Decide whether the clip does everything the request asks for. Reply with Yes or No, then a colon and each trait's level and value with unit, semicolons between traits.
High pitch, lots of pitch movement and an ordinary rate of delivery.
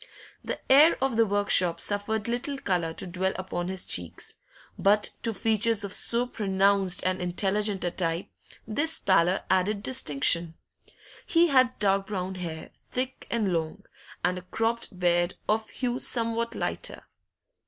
No: high, 200 Hz; average, 4.1 semitones; average, 150 wpm